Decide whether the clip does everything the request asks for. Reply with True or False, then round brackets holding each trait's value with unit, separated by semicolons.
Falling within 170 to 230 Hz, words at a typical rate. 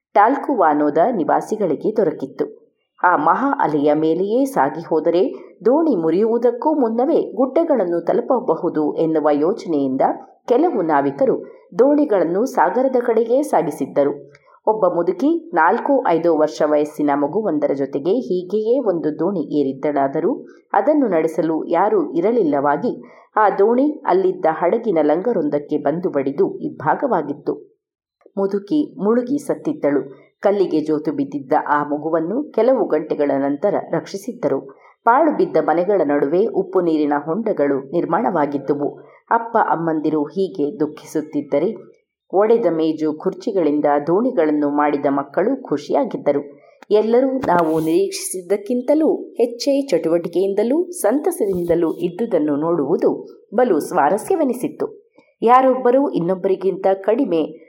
True (190 Hz; 95 wpm)